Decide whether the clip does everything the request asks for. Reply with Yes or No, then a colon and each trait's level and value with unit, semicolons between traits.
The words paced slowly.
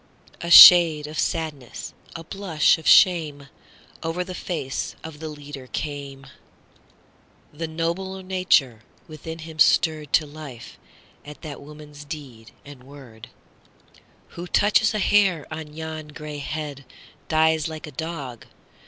Yes: slow, 115 wpm